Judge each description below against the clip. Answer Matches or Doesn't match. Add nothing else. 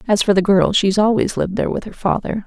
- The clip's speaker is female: Matches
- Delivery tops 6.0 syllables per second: Matches